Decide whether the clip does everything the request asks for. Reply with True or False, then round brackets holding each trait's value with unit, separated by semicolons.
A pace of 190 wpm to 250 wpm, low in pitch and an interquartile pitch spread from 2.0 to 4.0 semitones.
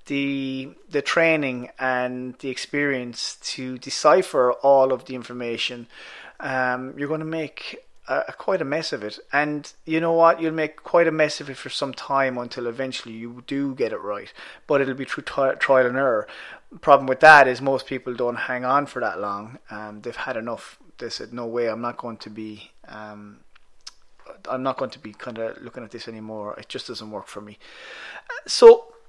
True (200 wpm; 130 Hz; 3.0 semitones)